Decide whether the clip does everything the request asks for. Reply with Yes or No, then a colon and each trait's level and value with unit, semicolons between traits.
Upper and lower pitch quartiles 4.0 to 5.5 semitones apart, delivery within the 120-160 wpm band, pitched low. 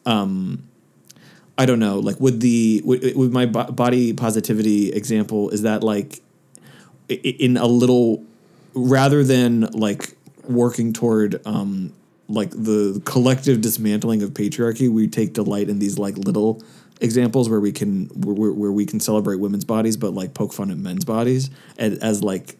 No: average, 3.1 semitones; average, 155 wpm; low, 110 Hz